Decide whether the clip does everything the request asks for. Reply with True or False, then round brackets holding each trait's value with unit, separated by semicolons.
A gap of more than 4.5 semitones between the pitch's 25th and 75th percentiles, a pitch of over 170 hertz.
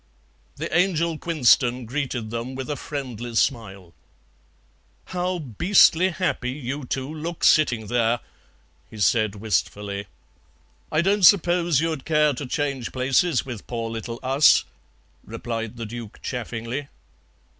False (5.1 semitones; 130 Hz)